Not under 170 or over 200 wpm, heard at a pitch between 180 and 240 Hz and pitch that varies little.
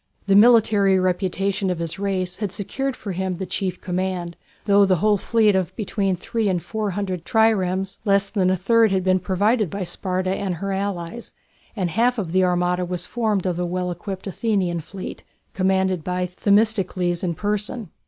Yes: average, 185 wpm; high, 190 Hz; narrow, 2.2 semitones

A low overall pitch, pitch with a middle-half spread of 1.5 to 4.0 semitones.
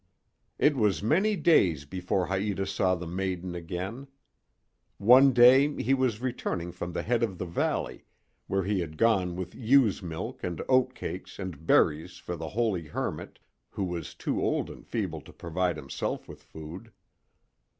No: very low, 95 Hz; average, 5.3 semitones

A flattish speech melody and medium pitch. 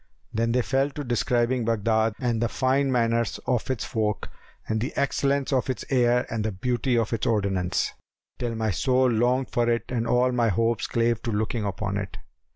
No: narrow, 2.3 semitones; low, 115 Hz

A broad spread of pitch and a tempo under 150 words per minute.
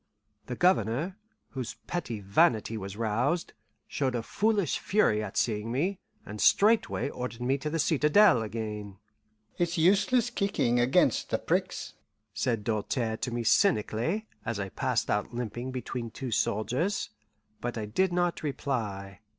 Yes: wide, 7.8 semitones; average, 140 wpm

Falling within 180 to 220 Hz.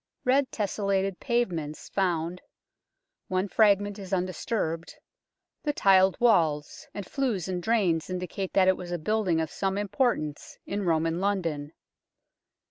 Yes: high, 190 Hz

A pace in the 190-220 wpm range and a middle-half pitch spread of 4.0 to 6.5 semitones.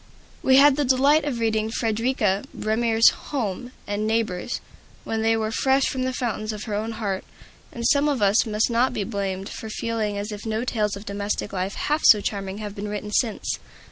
No: average, 200 wpm; average, 2.9 semitones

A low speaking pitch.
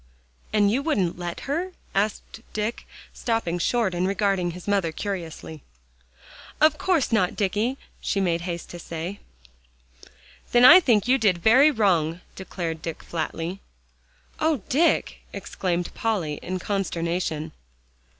No: high, 195 Hz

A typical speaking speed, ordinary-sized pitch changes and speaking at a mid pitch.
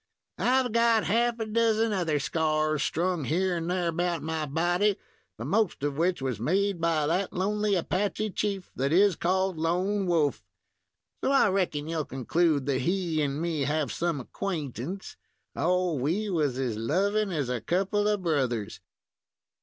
Yes: average, 160 wpm; average, 4.7 semitones; medium, 175 Hz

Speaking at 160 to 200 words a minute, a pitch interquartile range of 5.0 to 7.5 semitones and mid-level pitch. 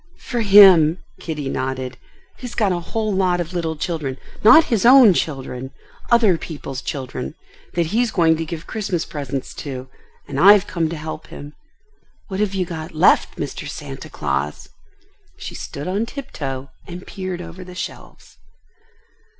No: average, 145 wpm; wide, 5.4 semitones; medium, 170 Hz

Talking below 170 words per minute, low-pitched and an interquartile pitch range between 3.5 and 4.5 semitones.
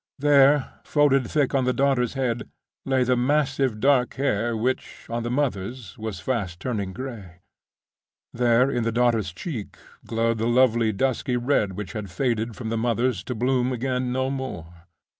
No: average, 160 wpm; low, 120 Hz; average, 3.1 semitones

